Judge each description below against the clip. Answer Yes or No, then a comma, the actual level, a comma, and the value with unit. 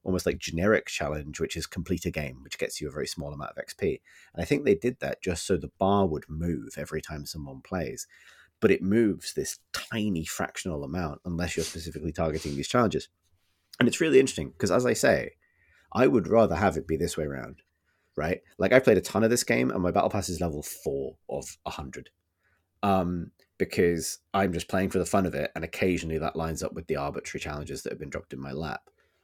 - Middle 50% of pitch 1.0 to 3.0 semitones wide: Yes, average, 2.7 semitones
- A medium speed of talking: No, fast, 225 wpm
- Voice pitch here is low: Yes, very low, 85 Hz